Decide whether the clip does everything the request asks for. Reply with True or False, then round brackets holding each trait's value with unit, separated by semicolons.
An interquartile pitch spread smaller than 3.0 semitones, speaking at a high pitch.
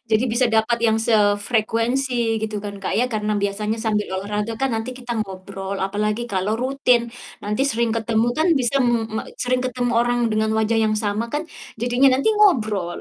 True (2.6 semitones; 220 Hz)